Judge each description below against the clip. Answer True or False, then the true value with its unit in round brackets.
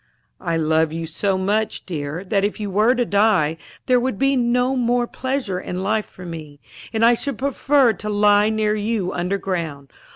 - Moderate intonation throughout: True (5.0 semitones)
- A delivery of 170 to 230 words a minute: True (185 wpm)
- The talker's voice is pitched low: False (205 Hz)